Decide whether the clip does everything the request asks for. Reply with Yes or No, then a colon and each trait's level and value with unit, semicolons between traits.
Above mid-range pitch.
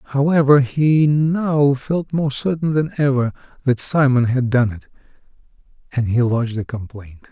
No: low, 135 Hz